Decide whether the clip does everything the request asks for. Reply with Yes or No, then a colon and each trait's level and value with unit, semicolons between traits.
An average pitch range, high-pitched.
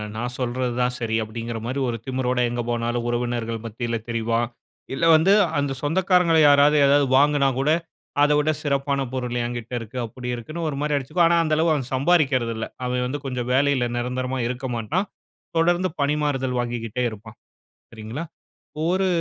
No: average, 3.6 semitones; low, 130 Hz